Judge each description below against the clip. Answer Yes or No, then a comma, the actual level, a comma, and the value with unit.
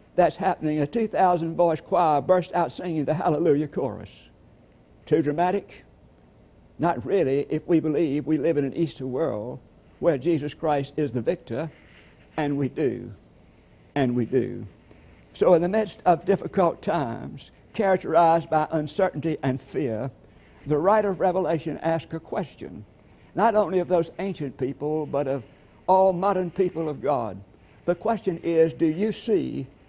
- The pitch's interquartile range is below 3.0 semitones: No, average, 4.1 semitones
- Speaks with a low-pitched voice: No, medium, 160 Hz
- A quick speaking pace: No, average, 155 wpm